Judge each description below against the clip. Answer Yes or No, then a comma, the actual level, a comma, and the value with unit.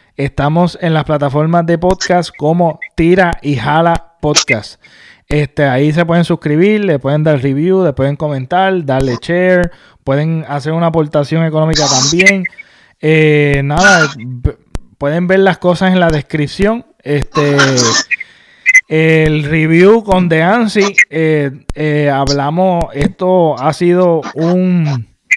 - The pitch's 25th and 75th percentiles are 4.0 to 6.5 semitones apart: No, average, 3.6 semitones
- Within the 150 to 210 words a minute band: No, slow, 125 wpm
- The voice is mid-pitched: Yes, medium, 160 Hz